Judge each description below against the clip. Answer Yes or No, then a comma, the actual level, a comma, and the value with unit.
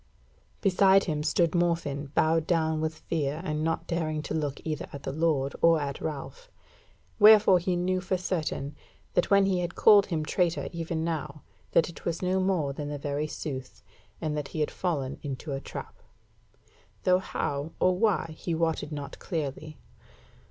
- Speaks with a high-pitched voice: No, medium, 160 Hz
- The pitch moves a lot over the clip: No, average, 3.3 semitones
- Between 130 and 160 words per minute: No, average, 175 wpm